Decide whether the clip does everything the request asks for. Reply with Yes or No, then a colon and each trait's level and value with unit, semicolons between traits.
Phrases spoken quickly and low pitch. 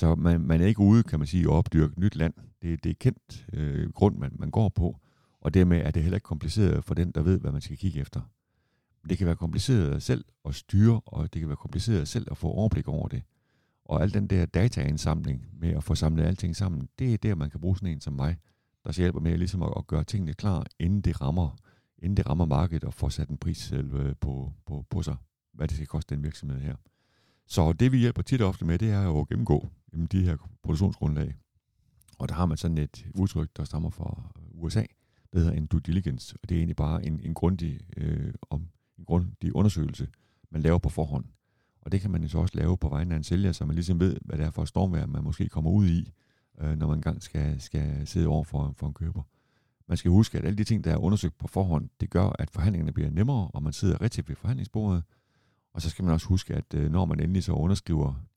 Yes: fast, 245 wpm; very low, 85 Hz